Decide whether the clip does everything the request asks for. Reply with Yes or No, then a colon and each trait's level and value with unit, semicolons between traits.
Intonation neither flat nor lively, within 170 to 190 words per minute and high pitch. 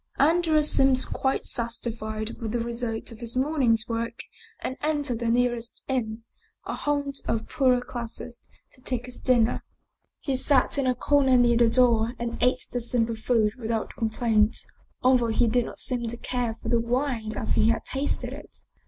No: narrow, 2.1 semitones; average, 180 wpm; high, 240 Hz